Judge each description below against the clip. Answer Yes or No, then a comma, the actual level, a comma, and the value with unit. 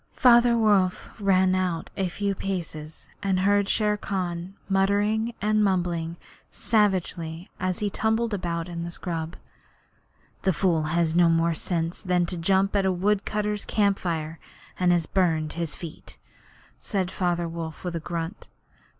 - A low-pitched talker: No, medium, 185 Hz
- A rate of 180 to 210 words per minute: No, average, 150 wpm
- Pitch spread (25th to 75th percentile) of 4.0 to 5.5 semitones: No, average, 3.0 semitones